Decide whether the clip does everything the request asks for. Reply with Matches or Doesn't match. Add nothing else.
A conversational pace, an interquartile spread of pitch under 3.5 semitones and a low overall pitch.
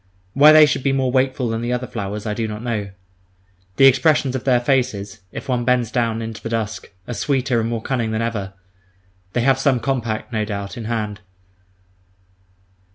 Matches